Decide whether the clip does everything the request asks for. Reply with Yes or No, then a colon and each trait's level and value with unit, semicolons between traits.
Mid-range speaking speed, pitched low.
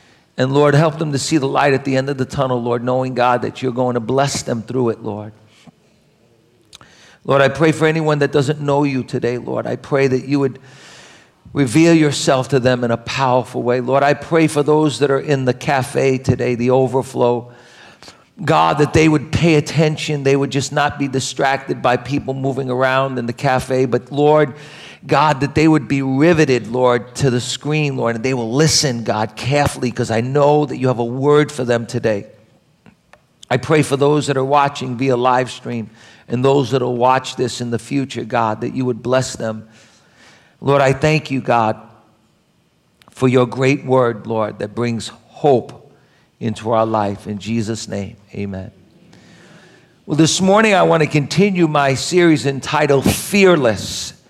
Yes: average, 185 wpm; low, 130 Hz